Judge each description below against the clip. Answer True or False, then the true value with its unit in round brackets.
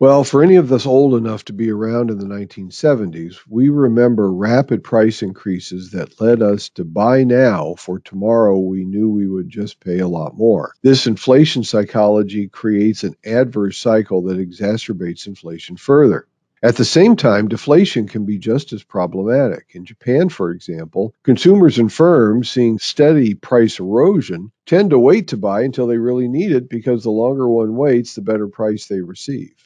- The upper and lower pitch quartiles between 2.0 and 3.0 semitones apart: False (4.0 semitones)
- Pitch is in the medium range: False (110 Hz)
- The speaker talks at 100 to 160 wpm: False (175 wpm)